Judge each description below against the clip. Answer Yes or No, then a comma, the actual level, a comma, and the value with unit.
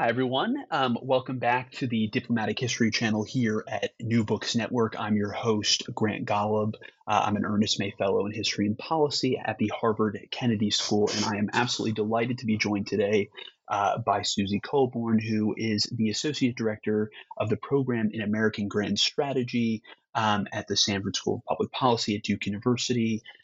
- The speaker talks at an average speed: Yes, average, 180 wpm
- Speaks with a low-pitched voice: Yes, low, 110 Hz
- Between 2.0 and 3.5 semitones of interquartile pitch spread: Yes, narrow, 2.5 semitones